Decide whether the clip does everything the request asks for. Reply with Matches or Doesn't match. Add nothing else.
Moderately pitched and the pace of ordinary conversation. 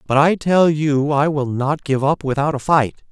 Doesn't match